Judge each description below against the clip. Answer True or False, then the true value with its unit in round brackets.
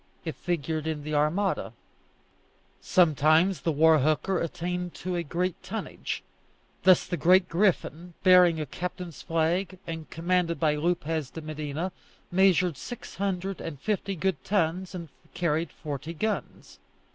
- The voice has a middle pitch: True (170 Hz)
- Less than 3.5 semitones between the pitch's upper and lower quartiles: True (2.7 semitones)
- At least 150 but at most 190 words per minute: False (135 wpm)